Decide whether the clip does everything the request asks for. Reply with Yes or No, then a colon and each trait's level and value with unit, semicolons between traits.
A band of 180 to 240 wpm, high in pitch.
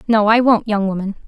Yes: fast, 235 wpm; high, 210 Hz